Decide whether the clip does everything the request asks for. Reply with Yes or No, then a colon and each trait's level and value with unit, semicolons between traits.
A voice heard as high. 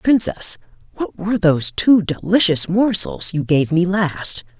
No: medium, 180 Hz